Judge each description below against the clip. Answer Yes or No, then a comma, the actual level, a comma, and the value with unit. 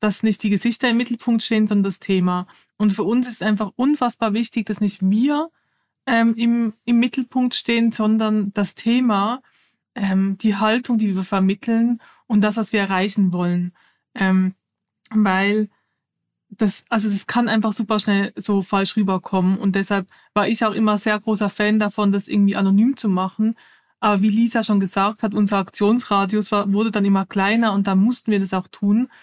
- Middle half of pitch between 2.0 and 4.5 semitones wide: Yes, narrow, 2.5 semitones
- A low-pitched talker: No, high, 210 Hz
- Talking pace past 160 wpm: Yes, average, 180 wpm